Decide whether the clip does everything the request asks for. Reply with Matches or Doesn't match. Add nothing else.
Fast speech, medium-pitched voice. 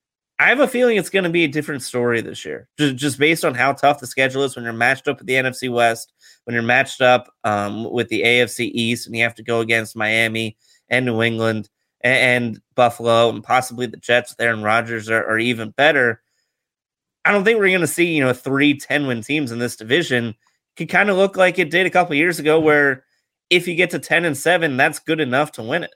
Doesn't match